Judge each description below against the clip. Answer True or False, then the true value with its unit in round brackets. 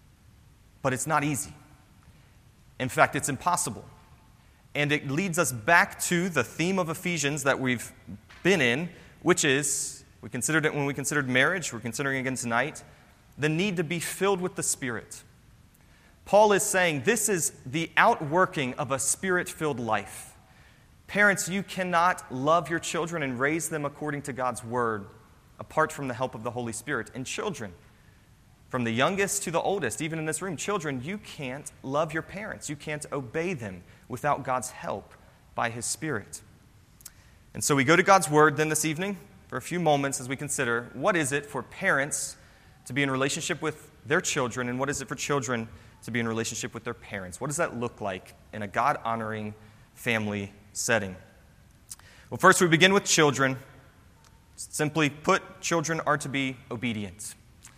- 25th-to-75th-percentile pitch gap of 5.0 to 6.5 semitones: True (5.5 semitones)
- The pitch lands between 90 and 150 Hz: True (140 Hz)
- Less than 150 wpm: False (175 wpm)